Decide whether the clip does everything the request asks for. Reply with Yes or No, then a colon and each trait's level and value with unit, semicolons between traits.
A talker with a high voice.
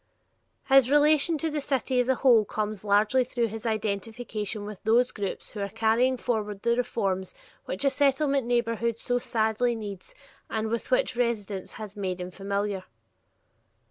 Yes: high, 225 Hz